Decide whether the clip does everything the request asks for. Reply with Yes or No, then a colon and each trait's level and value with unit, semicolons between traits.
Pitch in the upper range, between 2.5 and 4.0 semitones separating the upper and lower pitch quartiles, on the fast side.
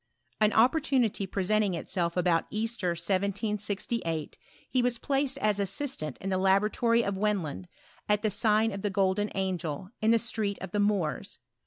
No: high, 205 Hz; average, 2.9 semitones; average, 155 wpm